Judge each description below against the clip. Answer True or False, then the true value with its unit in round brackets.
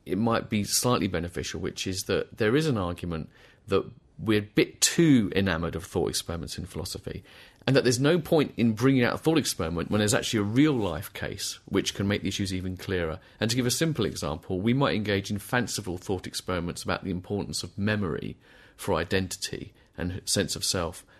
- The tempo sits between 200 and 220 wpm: True (205 wpm)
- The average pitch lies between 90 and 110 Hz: True (100 Hz)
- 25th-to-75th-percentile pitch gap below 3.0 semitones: False (4.3 semitones)